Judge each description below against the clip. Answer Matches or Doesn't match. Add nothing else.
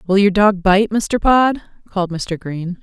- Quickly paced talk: Doesn't match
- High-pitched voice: Matches